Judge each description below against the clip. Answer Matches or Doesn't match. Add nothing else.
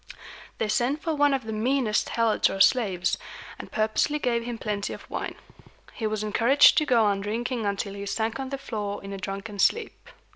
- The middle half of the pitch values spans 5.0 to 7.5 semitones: Doesn't match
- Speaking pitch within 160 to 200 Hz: Doesn't match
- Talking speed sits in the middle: Matches